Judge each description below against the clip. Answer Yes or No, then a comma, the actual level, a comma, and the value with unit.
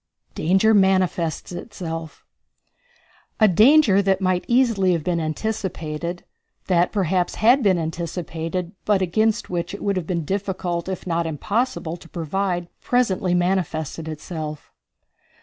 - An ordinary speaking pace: No, slow, 125 wpm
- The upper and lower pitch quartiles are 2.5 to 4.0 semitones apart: Yes, average, 3.0 semitones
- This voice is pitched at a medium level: Yes, medium, 180 Hz